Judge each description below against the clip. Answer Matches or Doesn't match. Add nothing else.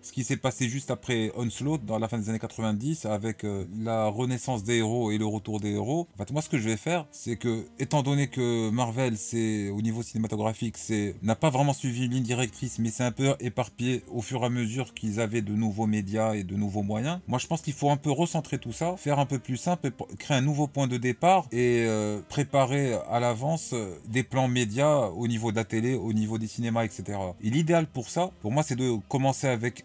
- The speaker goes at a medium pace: Doesn't match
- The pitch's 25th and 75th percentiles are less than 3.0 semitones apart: Doesn't match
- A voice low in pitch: Matches